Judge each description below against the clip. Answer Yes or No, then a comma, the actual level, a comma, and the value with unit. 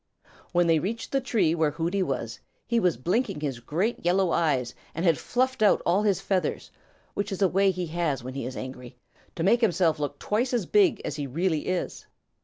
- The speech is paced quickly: Yes, fast, 210 wpm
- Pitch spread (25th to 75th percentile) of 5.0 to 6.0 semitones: Yes, average, 5.3 semitones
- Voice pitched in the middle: Yes, medium, 175 Hz